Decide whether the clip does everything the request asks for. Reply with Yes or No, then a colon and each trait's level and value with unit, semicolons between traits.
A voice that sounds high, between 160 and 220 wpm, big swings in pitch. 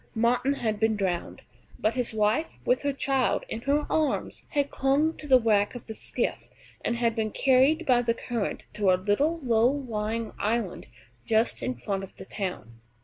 No: high, 230 Hz; average, 185 wpm; average, 4.2 semitones